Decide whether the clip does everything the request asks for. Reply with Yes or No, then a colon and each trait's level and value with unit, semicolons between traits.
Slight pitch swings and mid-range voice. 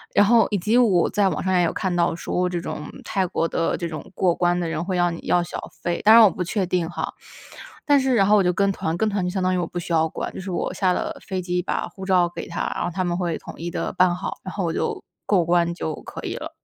Yes: narrow, 2.1 semitones; medium, 180 Hz